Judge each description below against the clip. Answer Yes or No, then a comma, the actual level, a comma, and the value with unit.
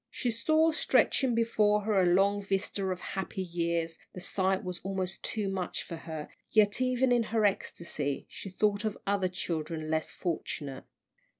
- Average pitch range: Yes, average, 3.7 semitones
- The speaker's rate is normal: Yes, average, 165 wpm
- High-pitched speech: Yes, high, 195 Hz